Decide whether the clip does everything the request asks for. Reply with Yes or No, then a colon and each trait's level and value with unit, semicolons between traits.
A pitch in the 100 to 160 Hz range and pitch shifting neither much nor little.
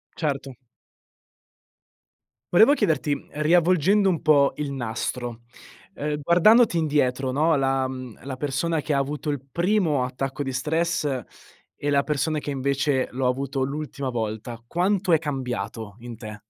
Yes: medium, 140 Hz; average, 3.6 semitones